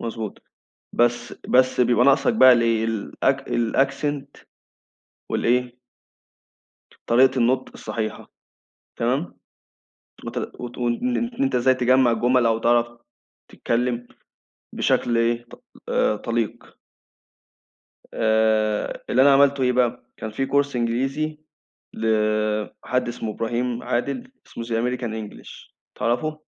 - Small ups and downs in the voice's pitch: Yes, narrow, 2.2 semitones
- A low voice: Yes, low, 120 Hz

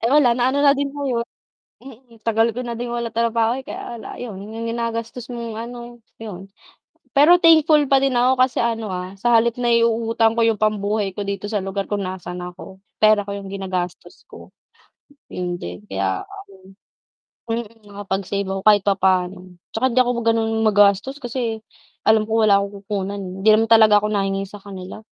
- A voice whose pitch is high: Yes, high, 220 Hz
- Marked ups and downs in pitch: No, average, 3.2 semitones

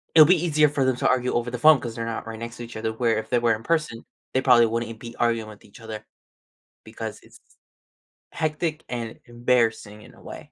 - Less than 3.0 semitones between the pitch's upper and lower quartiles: Yes, narrow, 2.5 semitones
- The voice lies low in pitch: Yes, low, 120 Hz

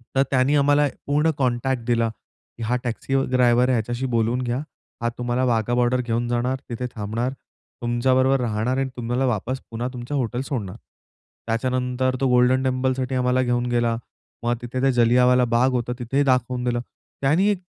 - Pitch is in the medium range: No, low, 125 Hz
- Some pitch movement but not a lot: No, narrow, 1.4 semitones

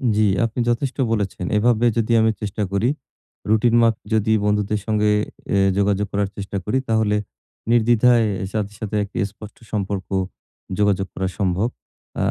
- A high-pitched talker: No, low, 105 Hz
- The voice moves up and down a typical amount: No, narrow, 1.9 semitones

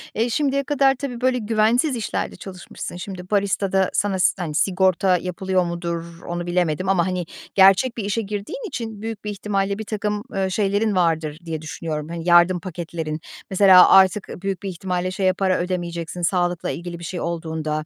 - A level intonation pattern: No, average, 3.2 semitones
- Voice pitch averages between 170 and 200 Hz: Yes, medium, 185 Hz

